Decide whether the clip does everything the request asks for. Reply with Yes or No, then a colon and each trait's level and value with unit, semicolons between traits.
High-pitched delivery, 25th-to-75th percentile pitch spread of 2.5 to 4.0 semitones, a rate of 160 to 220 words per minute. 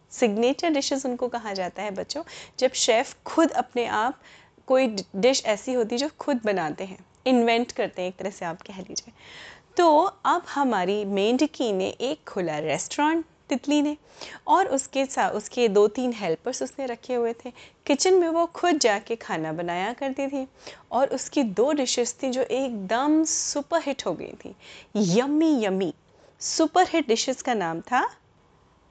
No: very high, 255 Hz; wide, 5.5 semitones; average, 165 wpm